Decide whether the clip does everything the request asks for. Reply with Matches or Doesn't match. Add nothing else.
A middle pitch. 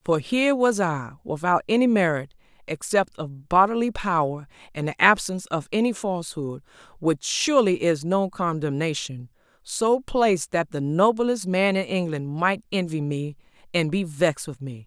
Matches